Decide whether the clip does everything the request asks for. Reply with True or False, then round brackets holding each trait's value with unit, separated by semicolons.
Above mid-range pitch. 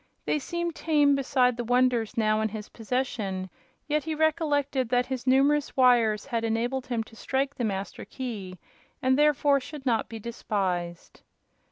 True (250 Hz)